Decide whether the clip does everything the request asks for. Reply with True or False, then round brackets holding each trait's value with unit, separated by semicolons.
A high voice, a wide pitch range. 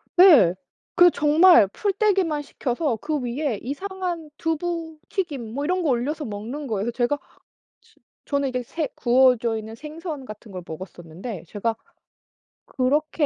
True (280 Hz; 6.0 semitones)